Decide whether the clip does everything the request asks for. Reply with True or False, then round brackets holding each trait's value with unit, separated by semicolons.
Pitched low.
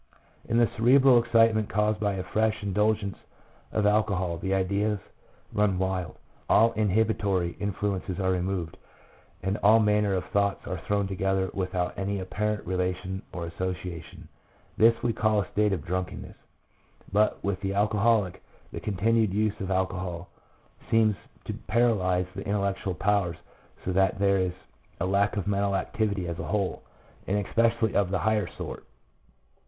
True (100 Hz)